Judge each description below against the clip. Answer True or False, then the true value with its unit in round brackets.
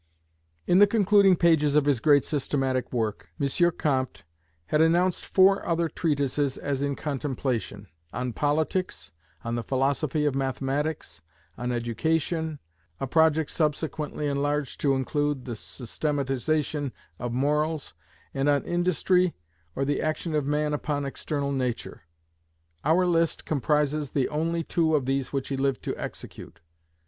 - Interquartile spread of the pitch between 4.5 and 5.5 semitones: False (3.0 semitones)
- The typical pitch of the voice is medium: True (145 Hz)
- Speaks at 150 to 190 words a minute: False (135 wpm)